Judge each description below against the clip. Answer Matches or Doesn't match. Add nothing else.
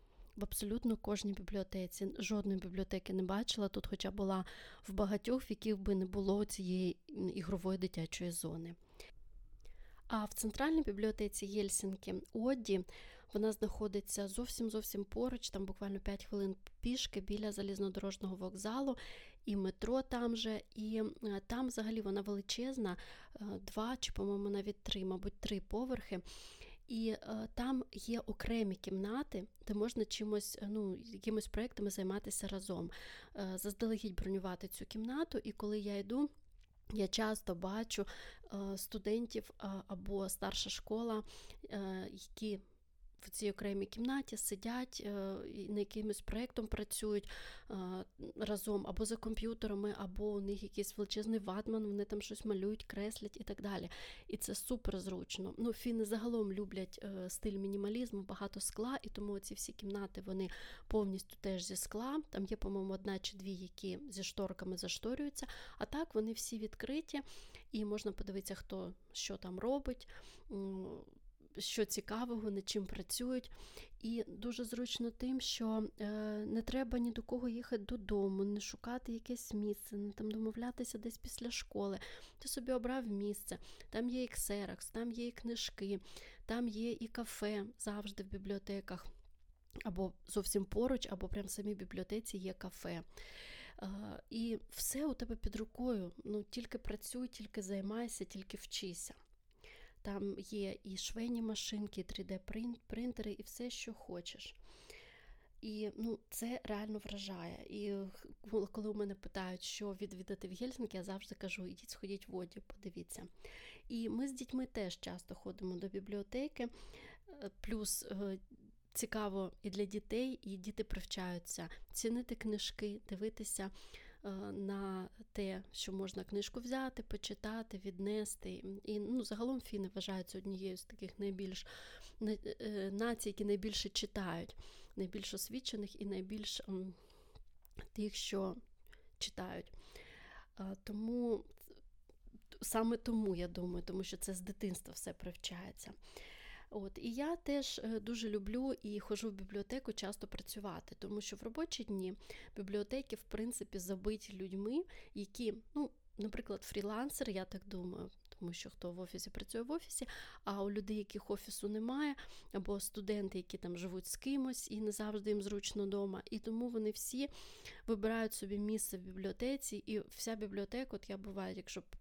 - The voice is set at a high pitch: Matches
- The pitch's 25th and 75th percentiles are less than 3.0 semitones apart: Matches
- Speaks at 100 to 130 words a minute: Doesn't match